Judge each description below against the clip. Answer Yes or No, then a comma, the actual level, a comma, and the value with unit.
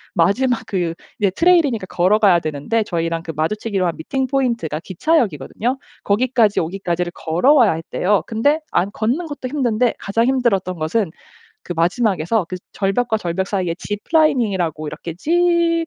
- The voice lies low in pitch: No, high, 205 Hz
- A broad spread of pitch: Yes, wide, 6.5 semitones